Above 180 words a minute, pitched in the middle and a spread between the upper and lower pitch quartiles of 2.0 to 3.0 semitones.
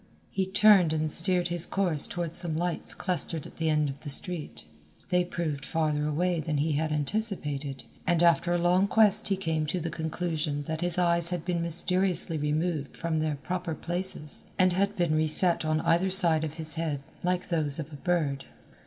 Yes: average, 190 wpm; medium, 165 Hz; narrow, 2.6 semitones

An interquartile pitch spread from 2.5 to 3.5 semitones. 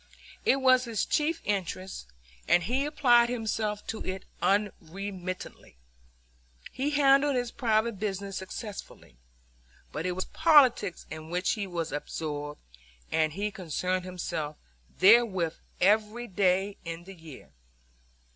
No: average, 5.0 semitones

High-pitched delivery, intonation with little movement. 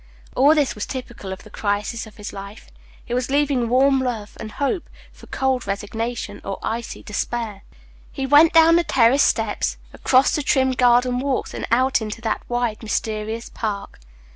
No: high, 240 Hz; average, 3.7 semitones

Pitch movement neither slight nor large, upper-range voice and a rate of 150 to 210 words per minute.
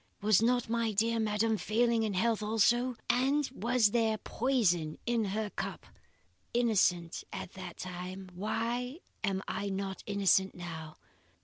No: average, 3.6 semitones; high, 215 Hz; slow, 135 wpm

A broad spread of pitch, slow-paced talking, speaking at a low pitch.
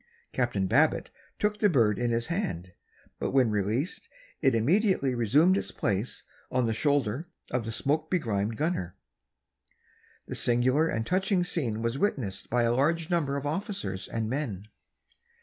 No: wide, 6.6 semitones; average, 150 wpm; low, 130 Hz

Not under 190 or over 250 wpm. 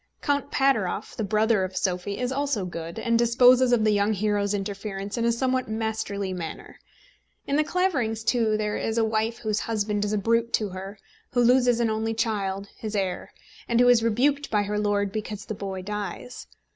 Yes: average, 195 wpm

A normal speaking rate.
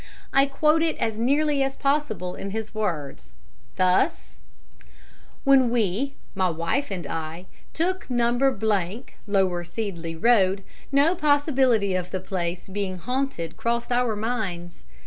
No: slow, 125 wpm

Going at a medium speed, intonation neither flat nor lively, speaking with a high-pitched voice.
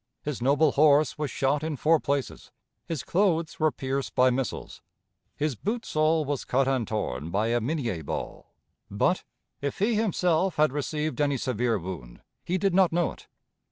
No: average, 170 wpm; average, 4.2 semitones; medium, 145 Hz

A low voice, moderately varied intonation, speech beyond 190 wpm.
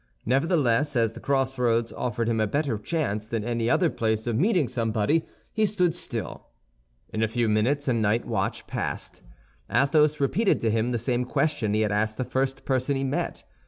No: low, 125 Hz; average, 4.2 semitones; average, 185 wpm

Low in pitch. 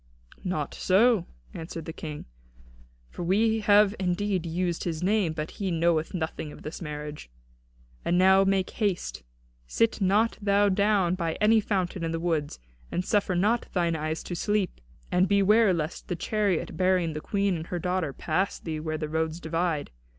No: medium, 180 Hz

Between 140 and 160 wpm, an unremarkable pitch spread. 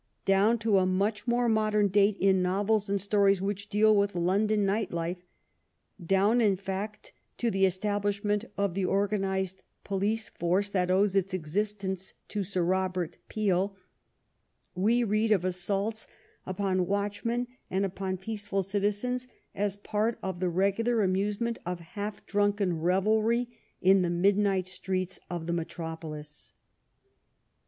No: average, 145 wpm; narrow, 2.0 semitones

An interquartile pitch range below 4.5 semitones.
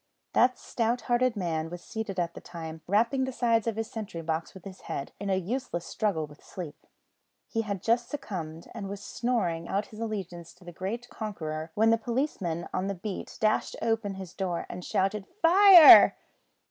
No: average, 4.8 semitones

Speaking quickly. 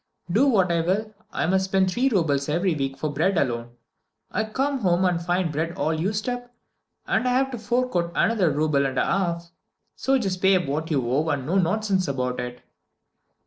Yes: fast, 210 wpm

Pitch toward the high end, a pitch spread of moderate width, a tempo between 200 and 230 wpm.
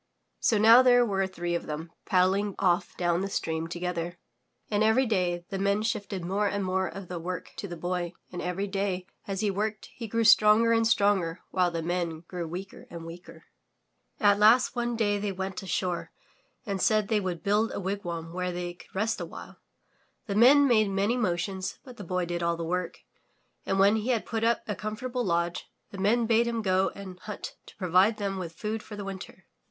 Yes: high, 195 Hz; average, 3.2 semitones; fast, 205 wpm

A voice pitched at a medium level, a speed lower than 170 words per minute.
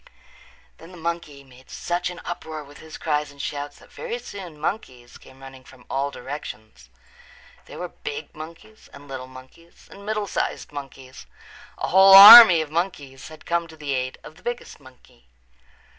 No: medium, 150 Hz; average, 175 wpm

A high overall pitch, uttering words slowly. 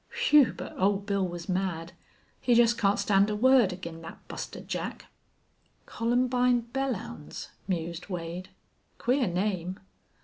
Yes: high, 200 Hz; slow, 130 wpm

